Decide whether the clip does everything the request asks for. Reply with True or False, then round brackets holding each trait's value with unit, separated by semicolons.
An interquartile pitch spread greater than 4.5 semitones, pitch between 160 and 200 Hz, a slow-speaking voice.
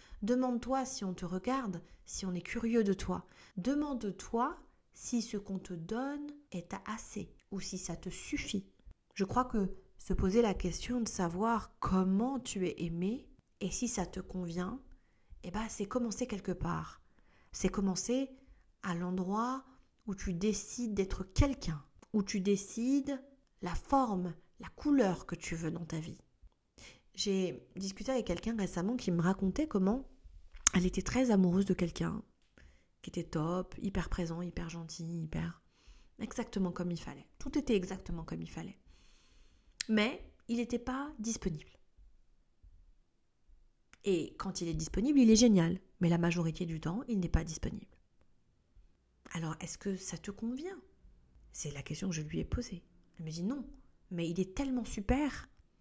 False (5.2 semitones; 190 Hz; 160 wpm)